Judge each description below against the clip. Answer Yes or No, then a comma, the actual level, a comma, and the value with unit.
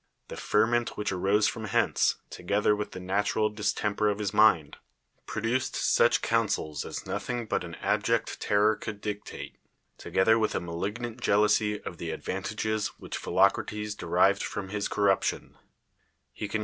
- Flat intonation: Yes, narrow, 1.8 semitones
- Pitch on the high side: No, low, 105 Hz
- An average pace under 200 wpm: Yes, average, 160 wpm